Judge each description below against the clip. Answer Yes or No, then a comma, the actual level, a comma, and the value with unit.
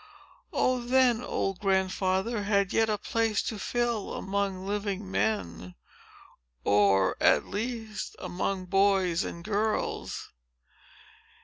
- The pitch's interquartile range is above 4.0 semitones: No, average, 3.0 semitones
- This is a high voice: Yes, high, 200 Hz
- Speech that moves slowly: Yes, slow, 100 wpm